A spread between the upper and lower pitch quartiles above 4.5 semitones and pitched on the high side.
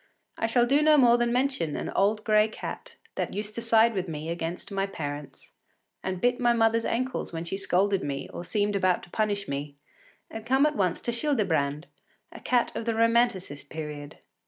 Yes: wide, 5.6 semitones; high, 210 Hz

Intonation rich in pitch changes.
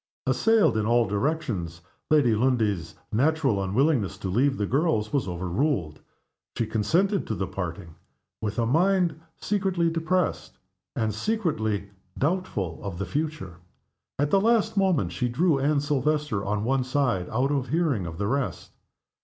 Yes: wide, 7.7 semitones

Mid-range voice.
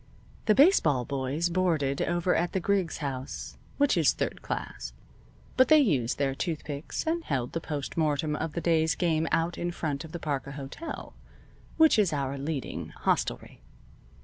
Yes: medium, 160 Hz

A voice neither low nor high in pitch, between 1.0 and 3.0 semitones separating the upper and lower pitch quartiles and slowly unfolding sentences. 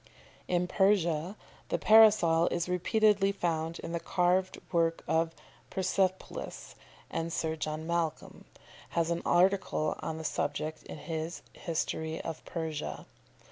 Yes: medium, 170 Hz; narrow, 2.5 semitones; slow, 130 wpm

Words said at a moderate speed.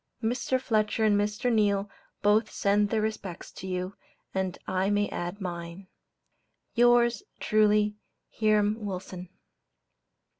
No: slow, 115 wpm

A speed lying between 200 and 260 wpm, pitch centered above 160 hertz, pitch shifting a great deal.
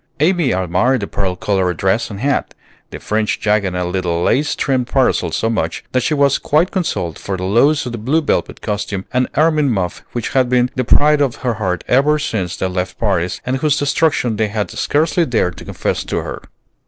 No: fast, 205 wpm; low, 120 Hz; wide, 6.7 semitones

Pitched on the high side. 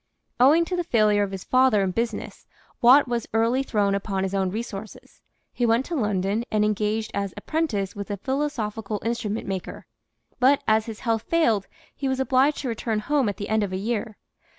Yes: high, 220 Hz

